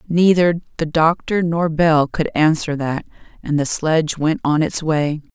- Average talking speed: Yes, average, 170 wpm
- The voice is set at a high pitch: No, medium, 160 Hz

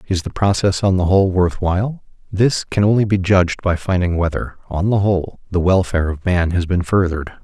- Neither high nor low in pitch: No, very low, 90 Hz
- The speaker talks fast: Yes, fast, 210 wpm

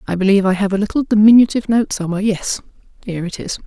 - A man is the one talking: No, female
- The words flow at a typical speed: No, fast, 215 wpm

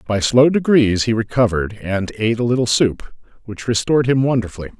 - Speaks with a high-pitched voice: No, low, 115 Hz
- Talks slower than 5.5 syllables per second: No, 6.0 syllables/s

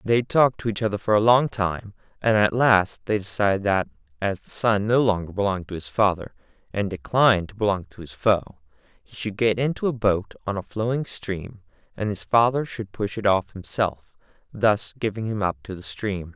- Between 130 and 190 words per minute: No, fast, 205 wpm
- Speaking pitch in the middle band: No, low, 105 Hz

